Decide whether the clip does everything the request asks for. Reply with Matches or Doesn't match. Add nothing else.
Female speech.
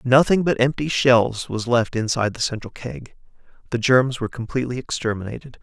Doesn't match